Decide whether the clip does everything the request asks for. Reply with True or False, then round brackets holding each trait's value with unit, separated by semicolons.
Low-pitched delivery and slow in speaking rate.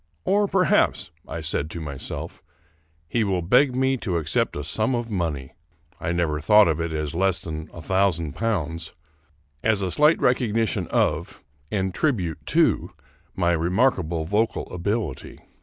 False (90 Hz; 155 wpm)